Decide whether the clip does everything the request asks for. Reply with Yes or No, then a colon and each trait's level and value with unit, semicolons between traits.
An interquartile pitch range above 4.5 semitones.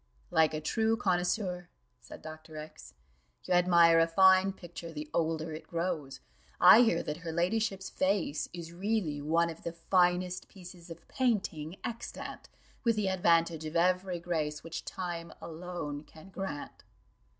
No: average, 2.7 semitones